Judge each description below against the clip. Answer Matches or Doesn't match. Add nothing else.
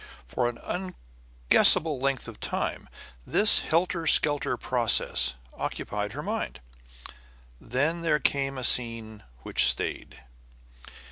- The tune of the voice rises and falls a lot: Matches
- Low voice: Matches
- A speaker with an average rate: Doesn't match